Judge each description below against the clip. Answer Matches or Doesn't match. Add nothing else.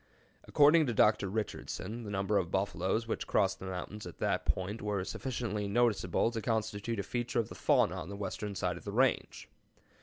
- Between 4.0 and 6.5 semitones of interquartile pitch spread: Doesn't match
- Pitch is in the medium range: Doesn't match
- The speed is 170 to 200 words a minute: Matches